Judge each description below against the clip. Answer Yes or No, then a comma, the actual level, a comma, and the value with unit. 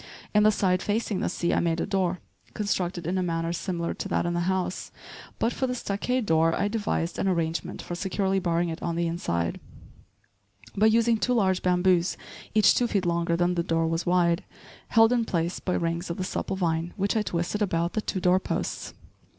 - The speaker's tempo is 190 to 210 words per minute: Yes, fast, 205 wpm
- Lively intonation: No, average, 3.1 semitones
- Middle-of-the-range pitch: Yes, medium, 180 Hz